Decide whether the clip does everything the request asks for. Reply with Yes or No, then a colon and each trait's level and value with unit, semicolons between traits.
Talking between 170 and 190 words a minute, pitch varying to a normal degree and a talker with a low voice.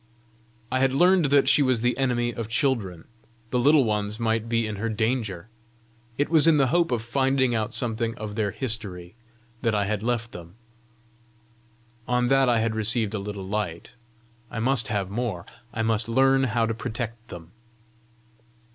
Yes: average, 175 wpm; average, 3.3 semitones; low, 115 Hz